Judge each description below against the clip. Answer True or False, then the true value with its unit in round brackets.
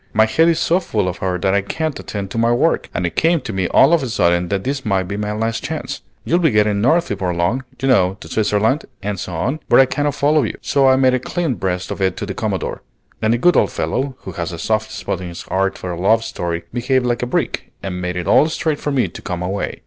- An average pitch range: False (6.1 semitones)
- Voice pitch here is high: False (110 Hz)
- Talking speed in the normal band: False (270 wpm)